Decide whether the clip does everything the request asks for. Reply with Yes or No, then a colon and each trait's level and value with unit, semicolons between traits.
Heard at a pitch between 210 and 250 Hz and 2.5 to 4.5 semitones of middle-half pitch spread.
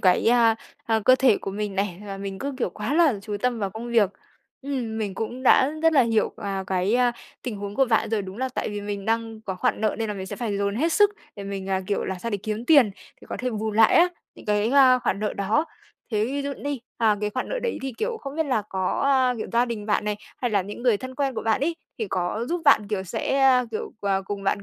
Yes: high, 220 Hz; average, 4.2 semitones